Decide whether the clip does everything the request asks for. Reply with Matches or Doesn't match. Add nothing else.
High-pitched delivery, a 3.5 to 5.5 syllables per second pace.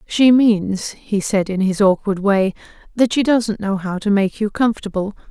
Matches